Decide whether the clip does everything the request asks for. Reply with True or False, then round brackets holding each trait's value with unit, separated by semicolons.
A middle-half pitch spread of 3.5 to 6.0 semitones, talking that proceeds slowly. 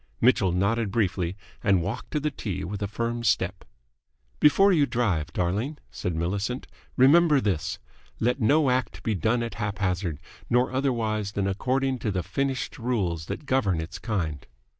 False (5.4 semitones; 160 wpm)